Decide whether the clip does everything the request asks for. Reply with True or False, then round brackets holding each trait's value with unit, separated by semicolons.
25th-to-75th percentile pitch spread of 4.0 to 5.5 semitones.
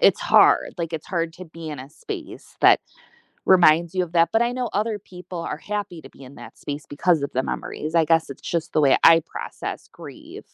False (3.0 semitones)